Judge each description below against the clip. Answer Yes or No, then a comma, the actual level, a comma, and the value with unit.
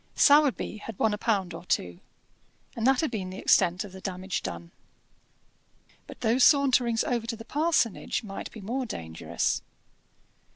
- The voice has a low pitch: No, high, 220 Hz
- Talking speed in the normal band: Yes, average, 160 wpm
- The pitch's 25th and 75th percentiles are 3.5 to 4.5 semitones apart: No, average, 5.1 semitones